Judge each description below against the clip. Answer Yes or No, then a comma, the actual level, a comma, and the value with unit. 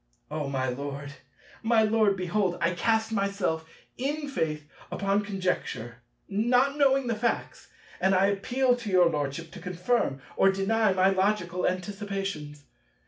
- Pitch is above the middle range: Yes, high, 195 Hz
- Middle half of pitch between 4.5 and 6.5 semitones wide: Yes, average, 4.8 semitones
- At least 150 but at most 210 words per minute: No, average, 140 wpm